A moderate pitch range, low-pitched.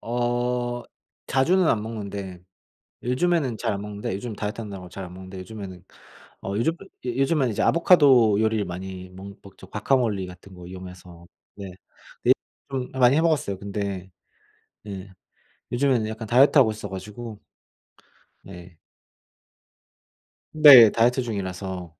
Yes: average, 4.4 semitones; low, 105 Hz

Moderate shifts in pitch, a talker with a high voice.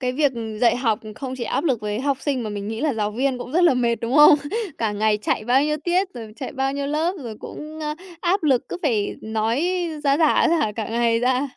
Yes: average, 5.0 semitones; very high, 255 Hz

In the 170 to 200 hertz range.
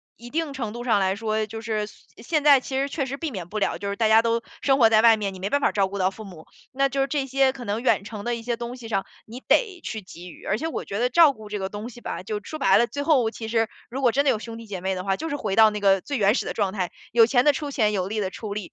No: high, 225 Hz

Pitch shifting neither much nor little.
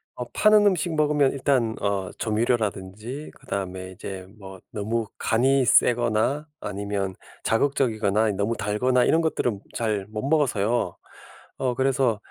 Yes: average, 4.9 semitones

